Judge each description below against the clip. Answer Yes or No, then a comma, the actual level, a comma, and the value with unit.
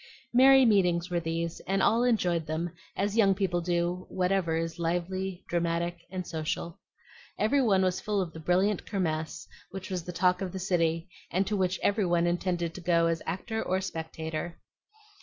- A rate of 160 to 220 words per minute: Yes, average, 175 wpm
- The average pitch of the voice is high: No, medium, 180 Hz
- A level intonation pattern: Yes, narrow, 2.3 semitones